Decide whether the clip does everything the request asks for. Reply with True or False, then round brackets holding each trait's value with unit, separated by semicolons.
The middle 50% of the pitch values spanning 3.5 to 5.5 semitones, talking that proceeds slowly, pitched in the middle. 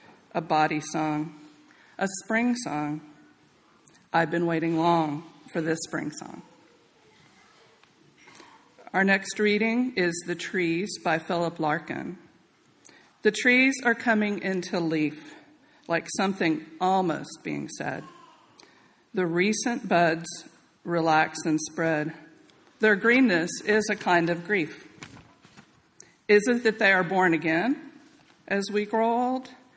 True (4.9 semitones; 115 wpm; 180 Hz)